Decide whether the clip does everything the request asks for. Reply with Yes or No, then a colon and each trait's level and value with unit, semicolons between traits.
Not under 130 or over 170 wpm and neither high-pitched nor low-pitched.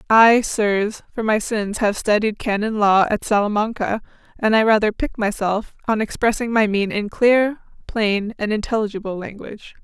No: average, 160 wpm; high, 215 Hz